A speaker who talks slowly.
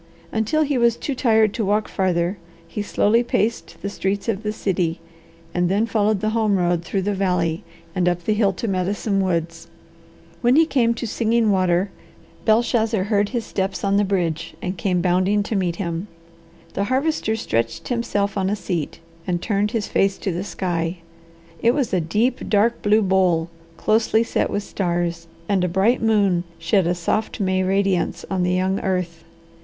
No: average, 180 wpm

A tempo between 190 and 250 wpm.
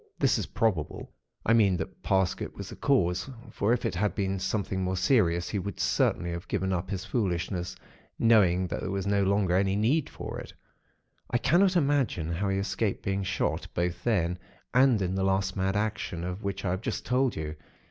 Yes: average, 200 wpm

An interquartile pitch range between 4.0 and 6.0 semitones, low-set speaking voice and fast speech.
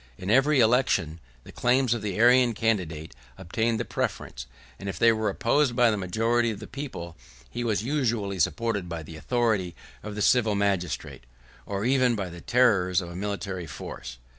No: average, 4.7 semitones; low, 105 Hz; average, 180 wpm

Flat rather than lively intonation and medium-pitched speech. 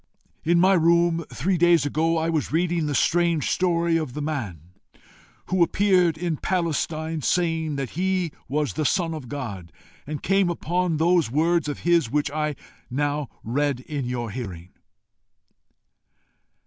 No: average, 3.1 semitones; medium, 160 Hz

